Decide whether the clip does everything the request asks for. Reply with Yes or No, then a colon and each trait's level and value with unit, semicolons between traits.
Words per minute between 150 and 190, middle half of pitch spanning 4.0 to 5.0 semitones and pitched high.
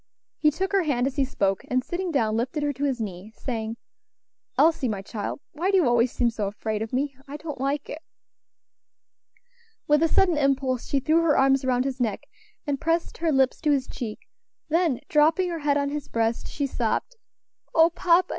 No: average, 200 wpm; average, 4.5 semitones; very high, 275 Hz